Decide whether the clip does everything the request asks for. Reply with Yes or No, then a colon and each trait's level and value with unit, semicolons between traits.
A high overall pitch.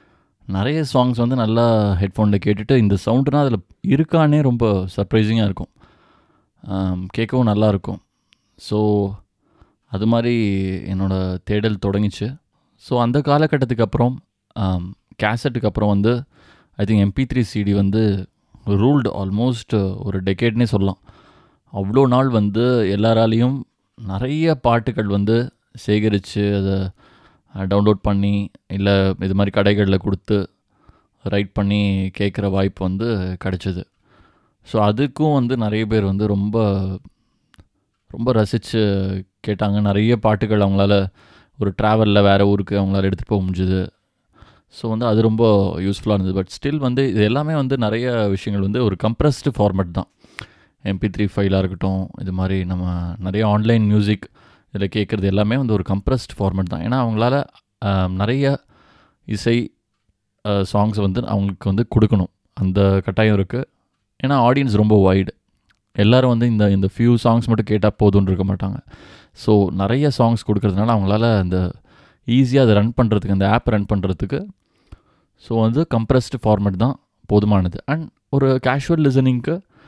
No: low, 105 Hz